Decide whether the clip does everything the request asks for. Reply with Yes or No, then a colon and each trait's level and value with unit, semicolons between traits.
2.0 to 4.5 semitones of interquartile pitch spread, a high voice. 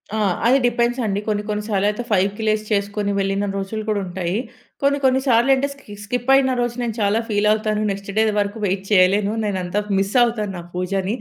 Yes: average, 2.7 semitones; high, 210 Hz